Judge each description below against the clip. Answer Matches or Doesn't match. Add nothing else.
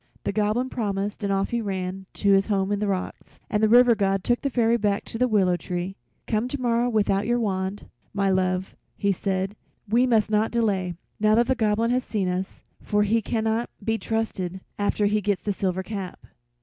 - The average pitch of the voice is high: Matches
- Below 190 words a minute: Doesn't match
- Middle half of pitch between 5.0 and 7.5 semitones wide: Doesn't match